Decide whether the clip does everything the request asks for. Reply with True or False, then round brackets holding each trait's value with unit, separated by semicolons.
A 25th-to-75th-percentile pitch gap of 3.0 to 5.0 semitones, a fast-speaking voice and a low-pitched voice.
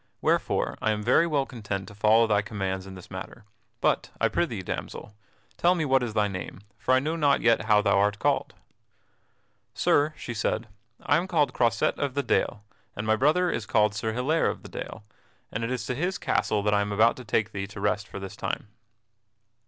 True (4.2 semitones; 215 wpm; 110 Hz)